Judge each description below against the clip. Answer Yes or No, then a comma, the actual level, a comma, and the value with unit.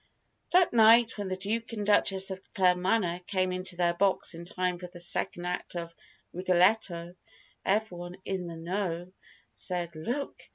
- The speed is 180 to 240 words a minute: No, average, 155 wpm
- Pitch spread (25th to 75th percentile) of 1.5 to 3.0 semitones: Yes, narrow, 2.5 semitones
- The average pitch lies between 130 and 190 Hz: Yes, medium, 185 Hz